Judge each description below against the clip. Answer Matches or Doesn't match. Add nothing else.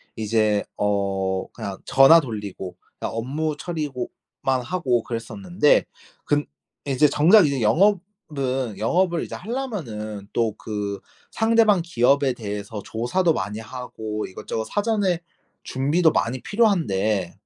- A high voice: Doesn't match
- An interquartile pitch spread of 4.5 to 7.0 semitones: Doesn't match